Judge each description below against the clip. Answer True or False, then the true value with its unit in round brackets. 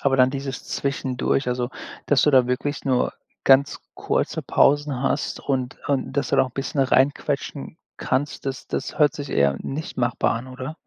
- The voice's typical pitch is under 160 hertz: True (135 Hz)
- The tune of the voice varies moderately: False (1.8 semitones)